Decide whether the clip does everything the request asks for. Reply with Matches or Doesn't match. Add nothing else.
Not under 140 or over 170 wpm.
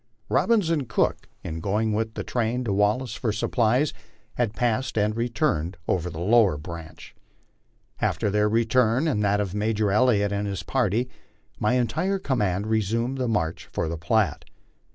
Matches